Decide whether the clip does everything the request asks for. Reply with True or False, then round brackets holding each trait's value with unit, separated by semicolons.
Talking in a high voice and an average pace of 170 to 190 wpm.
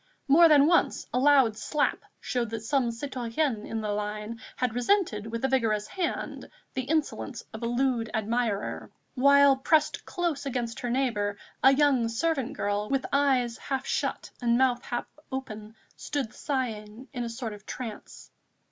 False (245 Hz; 160 wpm)